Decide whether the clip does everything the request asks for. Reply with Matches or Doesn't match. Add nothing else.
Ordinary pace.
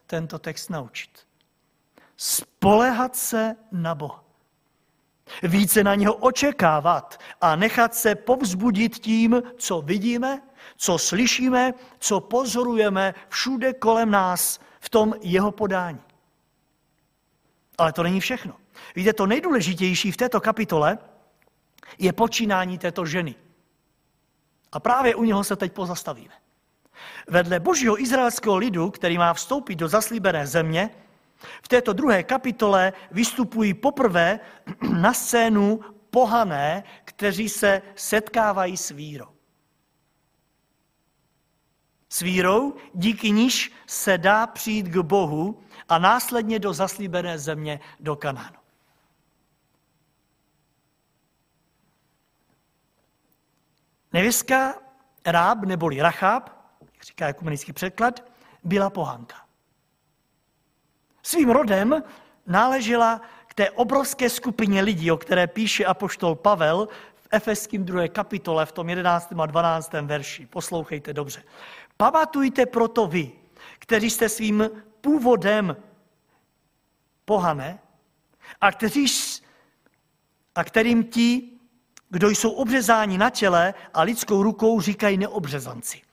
Doesn't match